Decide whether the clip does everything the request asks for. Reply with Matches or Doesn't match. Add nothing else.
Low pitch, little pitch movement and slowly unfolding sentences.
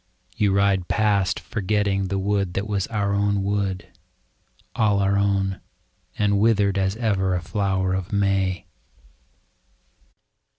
Matches